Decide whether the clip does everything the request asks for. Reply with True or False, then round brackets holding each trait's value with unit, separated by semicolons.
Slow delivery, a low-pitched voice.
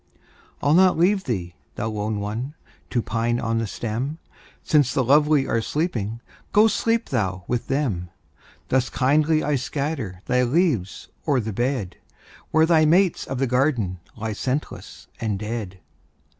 False (150 wpm; 125 Hz)